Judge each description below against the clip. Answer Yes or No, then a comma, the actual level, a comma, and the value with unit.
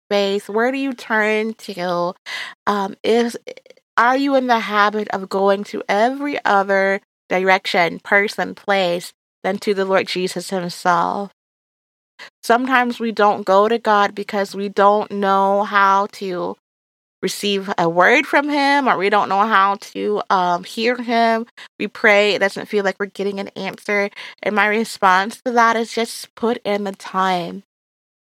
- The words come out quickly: No, average, 155 wpm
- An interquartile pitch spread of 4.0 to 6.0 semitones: No, average, 2.8 semitones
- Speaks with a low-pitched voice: No, high, 200 Hz